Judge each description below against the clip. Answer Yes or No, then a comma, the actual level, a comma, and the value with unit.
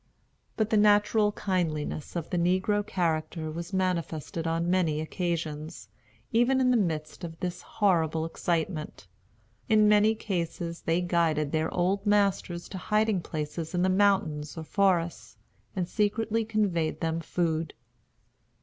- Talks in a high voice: No, medium, 175 Hz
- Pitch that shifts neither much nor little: Yes, average, 4.0 semitones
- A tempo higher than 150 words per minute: No, slow, 135 wpm